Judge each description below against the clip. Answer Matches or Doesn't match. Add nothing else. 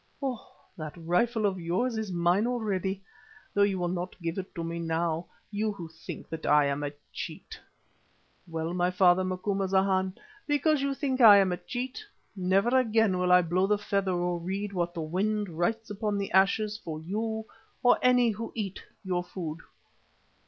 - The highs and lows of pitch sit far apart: Doesn't match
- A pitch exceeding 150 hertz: Matches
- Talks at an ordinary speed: Matches